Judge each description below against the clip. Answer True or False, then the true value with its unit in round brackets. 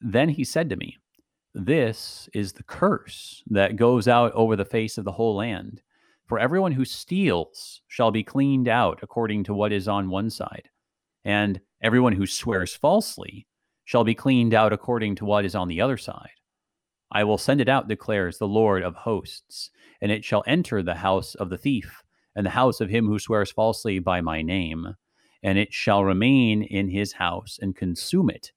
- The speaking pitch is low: True (105 Hz)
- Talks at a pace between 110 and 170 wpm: False (190 wpm)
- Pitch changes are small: False (3.1 semitones)